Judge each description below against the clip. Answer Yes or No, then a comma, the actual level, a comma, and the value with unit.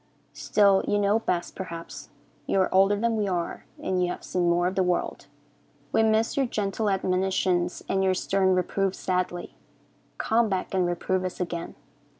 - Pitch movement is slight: Yes, narrow, 2.0 semitones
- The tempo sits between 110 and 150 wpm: No, average, 170 wpm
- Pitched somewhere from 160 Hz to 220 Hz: Yes, high, 190 Hz